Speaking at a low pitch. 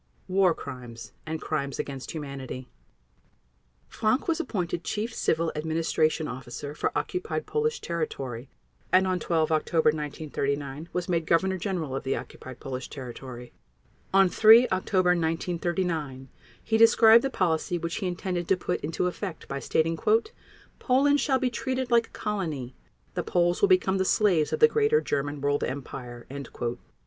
No: medium, 170 Hz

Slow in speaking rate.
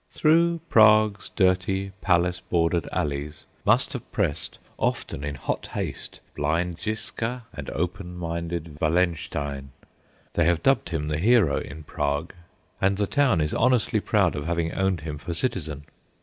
No: average, 145 wpm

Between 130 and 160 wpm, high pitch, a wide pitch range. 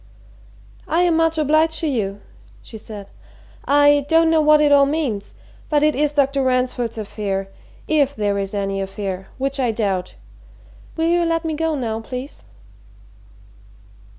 Yes: average, 150 wpm; very high, 275 Hz; wide, 6.6 semitones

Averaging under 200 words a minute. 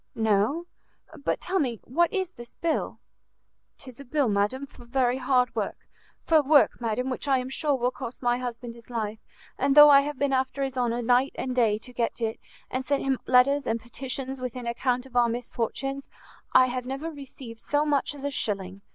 No: fast, 205 wpm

